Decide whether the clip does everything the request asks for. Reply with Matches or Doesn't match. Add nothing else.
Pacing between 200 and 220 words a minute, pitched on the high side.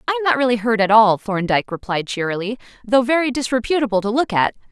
Matches